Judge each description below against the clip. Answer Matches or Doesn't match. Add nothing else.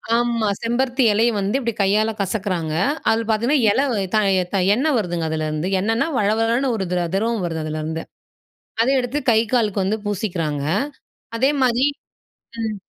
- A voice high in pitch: Matches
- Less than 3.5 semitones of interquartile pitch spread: Doesn't match